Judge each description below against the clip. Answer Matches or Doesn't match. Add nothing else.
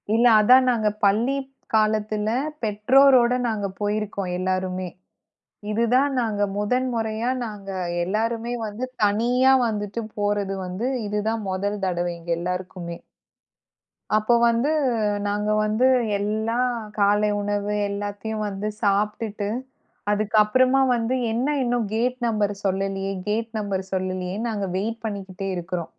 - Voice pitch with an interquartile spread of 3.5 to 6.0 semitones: Doesn't match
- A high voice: Matches